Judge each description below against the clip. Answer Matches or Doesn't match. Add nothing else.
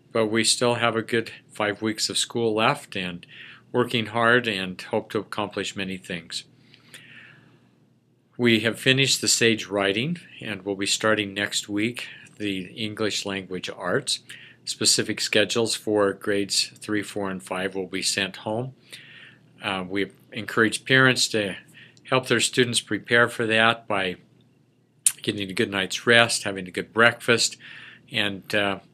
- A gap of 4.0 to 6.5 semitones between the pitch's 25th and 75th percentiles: Doesn't match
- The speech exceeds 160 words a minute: Doesn't match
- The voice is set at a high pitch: Doesn't match